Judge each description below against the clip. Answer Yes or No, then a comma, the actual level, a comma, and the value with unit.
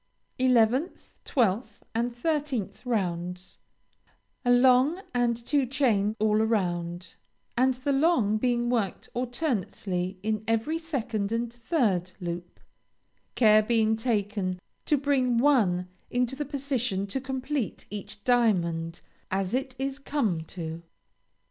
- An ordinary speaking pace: No, slow, 115 wpm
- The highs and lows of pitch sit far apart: No, average, 4.8 semitones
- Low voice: No, high, 230 Hz